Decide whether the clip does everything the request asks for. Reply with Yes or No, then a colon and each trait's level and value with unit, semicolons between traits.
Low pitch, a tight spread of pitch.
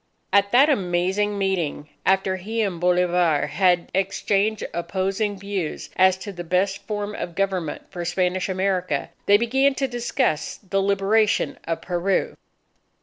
No: high, 190 Hz; narrow, 2.3 semitones